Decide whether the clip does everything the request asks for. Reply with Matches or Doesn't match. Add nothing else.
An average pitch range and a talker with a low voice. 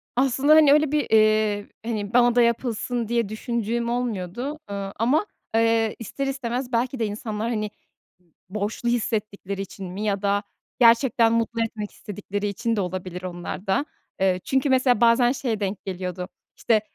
Doesn't match